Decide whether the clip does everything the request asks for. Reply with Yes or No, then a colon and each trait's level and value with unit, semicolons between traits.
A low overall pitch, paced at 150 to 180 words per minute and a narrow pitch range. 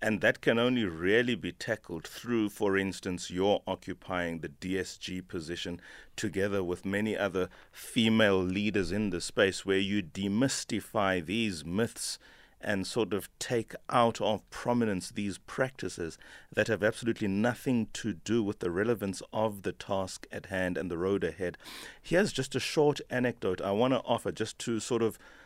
No: low, 105 Hz; average, 165 wpm; average, 3.4 semitones